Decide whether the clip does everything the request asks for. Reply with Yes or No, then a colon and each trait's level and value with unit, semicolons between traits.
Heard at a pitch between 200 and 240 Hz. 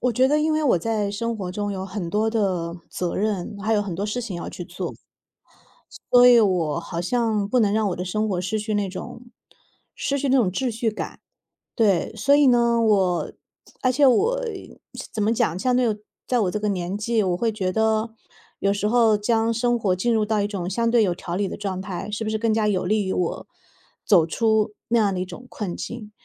Yes: high, 210 Hz